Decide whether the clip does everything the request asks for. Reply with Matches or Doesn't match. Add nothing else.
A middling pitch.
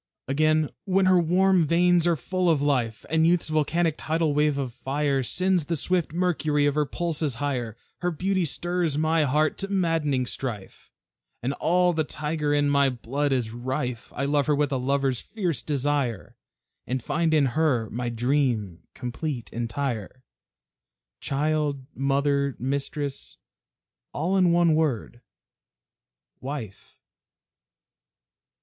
Matches